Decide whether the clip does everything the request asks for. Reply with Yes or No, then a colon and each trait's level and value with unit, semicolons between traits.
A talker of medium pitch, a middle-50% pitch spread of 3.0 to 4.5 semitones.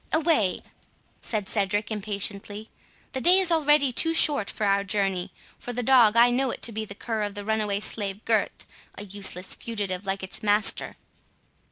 No: high, 215 Hz; average, 3.5 semitones